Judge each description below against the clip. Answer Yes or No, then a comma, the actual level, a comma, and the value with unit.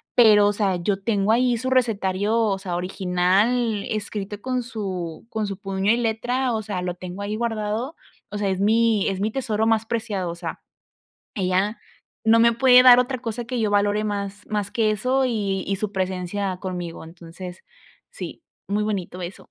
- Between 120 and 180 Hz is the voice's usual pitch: No, high, 205 Hz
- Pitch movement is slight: No, average, 3.1 semitones